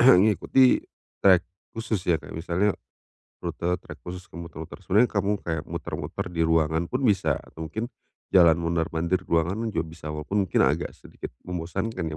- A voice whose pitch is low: Yes, very low, 85 Hz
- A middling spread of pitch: Yes, average, 3.7 semitones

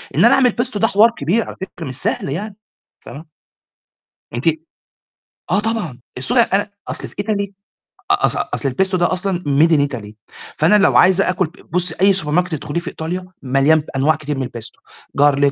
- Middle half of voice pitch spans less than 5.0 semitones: No, wide, 5.5 semitones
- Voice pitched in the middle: Yes, medium, 170 Hz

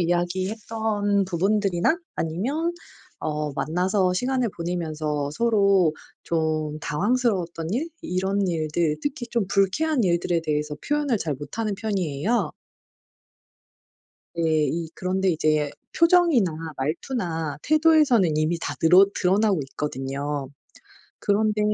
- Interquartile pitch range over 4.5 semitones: Yes, wide, 5.6 semitones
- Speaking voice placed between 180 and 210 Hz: Yes, medium, 185 Hz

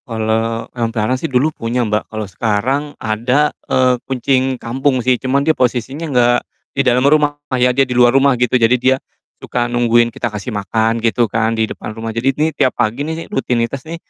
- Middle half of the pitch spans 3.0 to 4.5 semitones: No, narrow, 2.6 semitones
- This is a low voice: Yes, low, 125 Hz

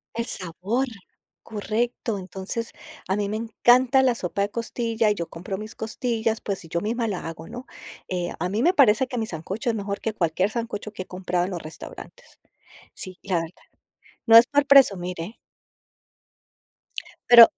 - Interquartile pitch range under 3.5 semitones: No, average, 4.2 semitones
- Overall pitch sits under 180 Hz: No, high, 210 Hz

